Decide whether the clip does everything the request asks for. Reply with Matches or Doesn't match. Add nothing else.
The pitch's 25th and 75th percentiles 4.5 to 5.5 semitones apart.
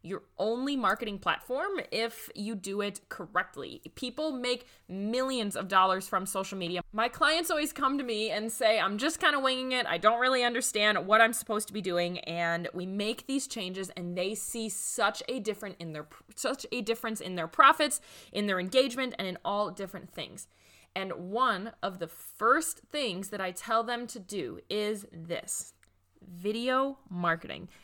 Matches